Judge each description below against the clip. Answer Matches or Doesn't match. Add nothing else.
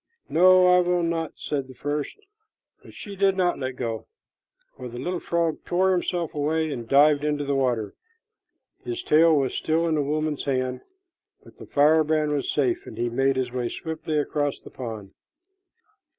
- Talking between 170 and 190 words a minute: Matches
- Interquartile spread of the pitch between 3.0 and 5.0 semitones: Matches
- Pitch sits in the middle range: Matches